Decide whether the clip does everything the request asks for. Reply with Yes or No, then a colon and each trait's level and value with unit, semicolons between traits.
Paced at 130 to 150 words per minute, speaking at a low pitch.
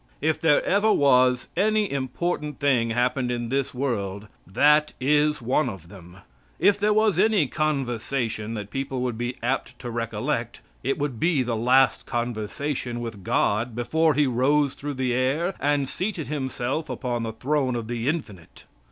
No: average, 160 wpm; low, 130 Hz